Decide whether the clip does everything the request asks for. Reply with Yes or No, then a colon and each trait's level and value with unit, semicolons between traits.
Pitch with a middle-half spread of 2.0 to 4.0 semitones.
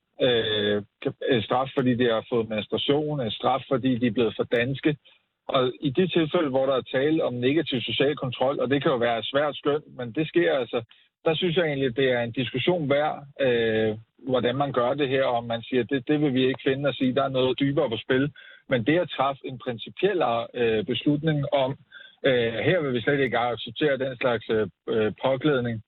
Yes: average, 3.3 semitones